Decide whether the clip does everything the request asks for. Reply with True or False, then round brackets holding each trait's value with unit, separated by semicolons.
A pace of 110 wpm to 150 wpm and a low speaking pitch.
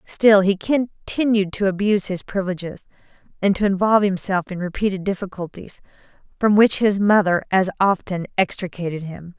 False (140 wpm; 195 Hz)